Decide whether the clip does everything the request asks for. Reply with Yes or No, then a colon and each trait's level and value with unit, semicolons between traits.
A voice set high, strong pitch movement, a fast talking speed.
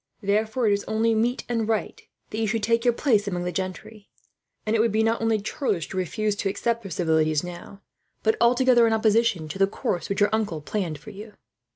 No: high, 215 Hz; average, 3.0 semitones; fast, 220 wpm